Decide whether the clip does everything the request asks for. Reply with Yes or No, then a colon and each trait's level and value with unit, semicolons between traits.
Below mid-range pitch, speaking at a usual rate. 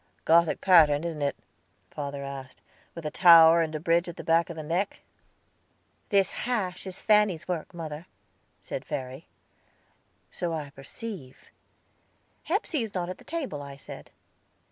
No: medium, 165 Hz; average, 150 wpm